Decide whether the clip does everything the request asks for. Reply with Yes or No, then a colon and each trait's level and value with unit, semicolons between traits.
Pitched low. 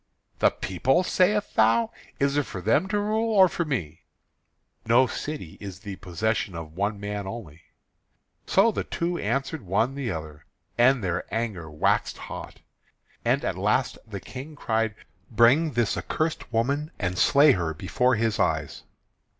Yes: low, 115 Hz